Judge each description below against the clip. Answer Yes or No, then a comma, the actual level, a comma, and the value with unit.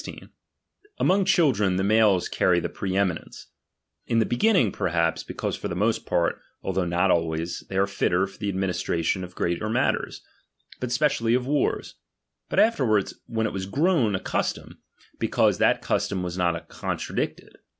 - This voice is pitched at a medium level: No, low, 100 Hz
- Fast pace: No, average, 165 wpm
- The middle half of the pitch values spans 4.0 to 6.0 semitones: Yes, average, 4.4 semitones